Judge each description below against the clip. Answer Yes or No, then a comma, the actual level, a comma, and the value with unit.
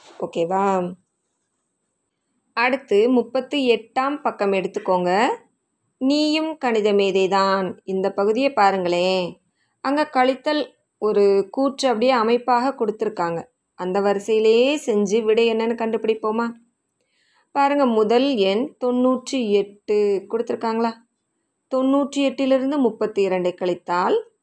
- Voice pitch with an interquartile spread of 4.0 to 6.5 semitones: Yes, average, 4.7 semitones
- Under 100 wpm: Yes, average, 90 wpm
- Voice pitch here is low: No, high, 230 Hz